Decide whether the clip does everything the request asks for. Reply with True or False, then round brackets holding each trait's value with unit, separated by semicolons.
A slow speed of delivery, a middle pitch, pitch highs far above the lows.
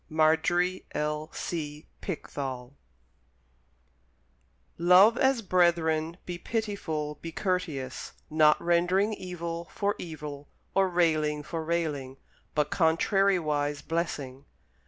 False (95 wpm; 165 Hz; 3.1 semitones)